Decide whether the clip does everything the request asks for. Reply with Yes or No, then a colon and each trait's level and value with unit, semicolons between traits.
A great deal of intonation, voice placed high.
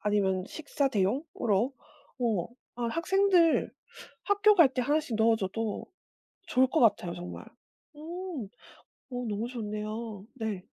Yes: wide, 6.5 semitones; high, 235 Hz